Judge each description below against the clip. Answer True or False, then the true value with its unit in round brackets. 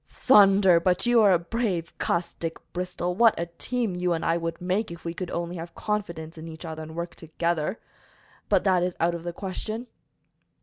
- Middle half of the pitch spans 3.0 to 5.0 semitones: False (2.6 semitones)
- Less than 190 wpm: False (205 wpm)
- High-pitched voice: False (175 Hz)